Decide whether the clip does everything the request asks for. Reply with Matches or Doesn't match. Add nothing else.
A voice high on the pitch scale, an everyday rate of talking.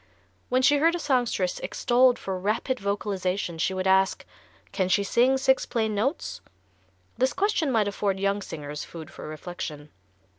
Matches